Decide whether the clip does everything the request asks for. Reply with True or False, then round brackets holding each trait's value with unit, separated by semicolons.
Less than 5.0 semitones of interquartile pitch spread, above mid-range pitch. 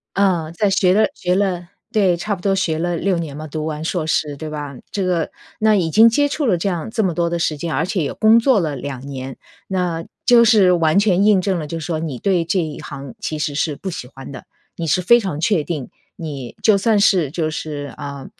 False (4.2 semitones; 170 Hz)